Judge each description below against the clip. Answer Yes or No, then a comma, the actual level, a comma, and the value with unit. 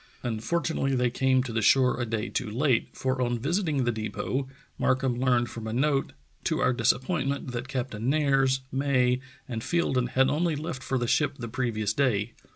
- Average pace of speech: Yes, average, 180 wpm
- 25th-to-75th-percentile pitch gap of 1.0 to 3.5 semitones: Yes, narrow, 2.4 semitones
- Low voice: Yes, low, 130 Hz